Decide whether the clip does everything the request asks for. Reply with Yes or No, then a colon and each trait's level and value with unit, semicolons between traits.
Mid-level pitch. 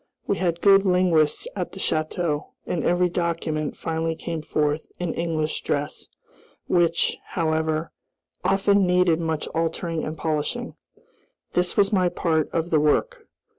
Yes: medium, 165 Hz